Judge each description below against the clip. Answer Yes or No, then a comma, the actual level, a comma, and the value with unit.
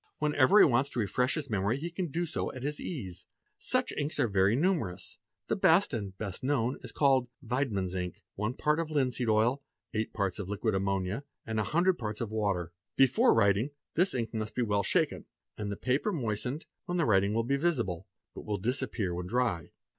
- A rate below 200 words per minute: No, fast, 205 wpm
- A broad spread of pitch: Yes, wide, 5.8 semitones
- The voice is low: Yes, low, 120 Hz